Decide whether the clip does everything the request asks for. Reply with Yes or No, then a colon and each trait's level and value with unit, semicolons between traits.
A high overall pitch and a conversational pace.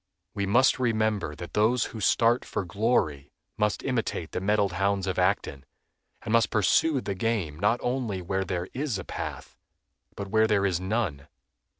No: low, 100 Hz; average, 170 wpm